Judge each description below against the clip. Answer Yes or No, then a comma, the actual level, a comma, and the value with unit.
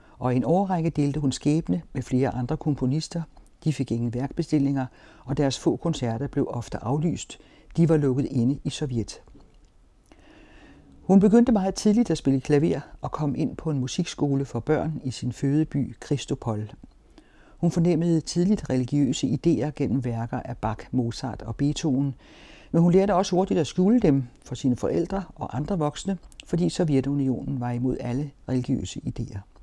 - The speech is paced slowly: No, average, 160 wpm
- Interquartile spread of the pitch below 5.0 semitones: Yes, average, 4.4 semitones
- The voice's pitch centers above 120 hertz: Yes, medium, 140 Hz